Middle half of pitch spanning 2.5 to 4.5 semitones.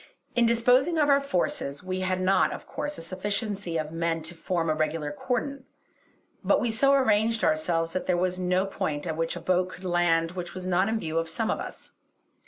No: average, 5.1 semitones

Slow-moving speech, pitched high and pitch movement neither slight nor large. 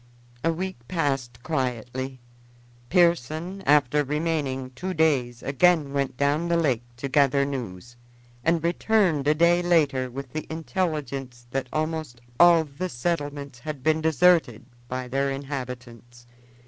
No: slow, 130 wpm; medium, 145 Hz; average, 4.2 semitones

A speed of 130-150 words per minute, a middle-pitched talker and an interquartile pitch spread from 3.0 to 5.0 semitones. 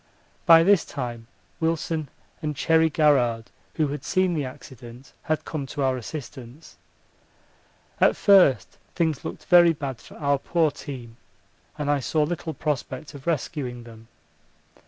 Yes: average, 140 wpm; medium, 145 Hz; average, 4.0 semitones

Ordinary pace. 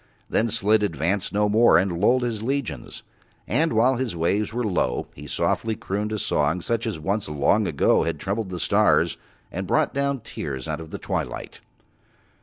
Yes: average, 180 wpm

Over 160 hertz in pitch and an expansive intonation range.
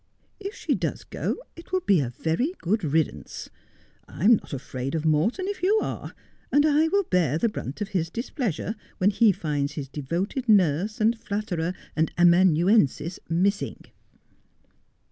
Yes: medium, 185 Hz; wide, 6.3 semitones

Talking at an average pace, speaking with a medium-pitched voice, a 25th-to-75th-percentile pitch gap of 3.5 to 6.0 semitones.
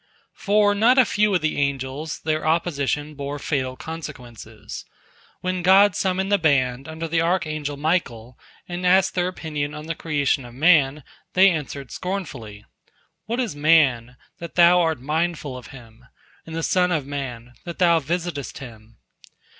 Yes: average, 160 wpm; medium, 155 Hz; average, 4.7 semitones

